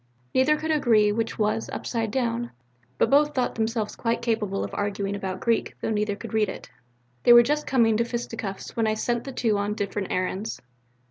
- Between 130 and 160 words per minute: No, average, 195 wpm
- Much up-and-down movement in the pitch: No, narrow, 2.4 semitones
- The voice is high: Yes, high, 225 Hz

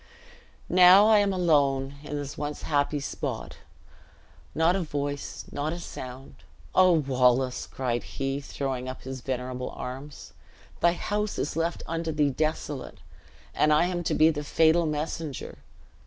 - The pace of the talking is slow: No, average, 145 wpm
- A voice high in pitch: No, medium, 150 Hz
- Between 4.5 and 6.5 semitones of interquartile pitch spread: No, average, 3.6 semitones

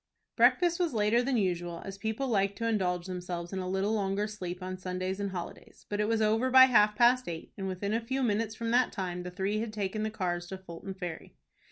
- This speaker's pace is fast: Yes, fast, 230 wpm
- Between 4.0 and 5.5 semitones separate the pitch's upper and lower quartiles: No, average, 3.4 semitones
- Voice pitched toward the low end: No, high, 200 Hz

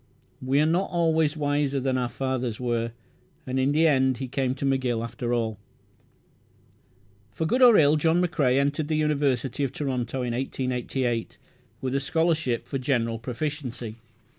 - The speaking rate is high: No, average, 160 wpm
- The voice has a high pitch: No, low, 135 Hz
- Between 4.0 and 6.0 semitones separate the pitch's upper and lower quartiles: No, average, 3.4 semitones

